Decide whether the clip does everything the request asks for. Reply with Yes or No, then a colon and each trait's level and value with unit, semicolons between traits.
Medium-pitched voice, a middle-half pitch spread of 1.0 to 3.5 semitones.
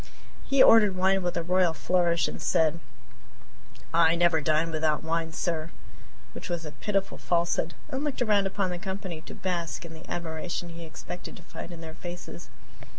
Yes: medium, 170 Hz; narrow, 2.4 semitones